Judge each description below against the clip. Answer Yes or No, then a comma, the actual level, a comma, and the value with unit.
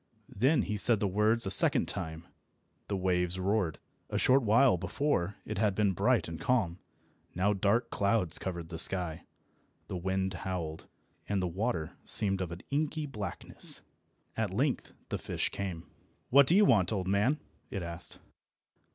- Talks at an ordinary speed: Yes, average, 160 wpm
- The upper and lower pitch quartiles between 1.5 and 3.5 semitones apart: No, average, 4.1 semitones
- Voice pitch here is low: Yes, low, 100 Hz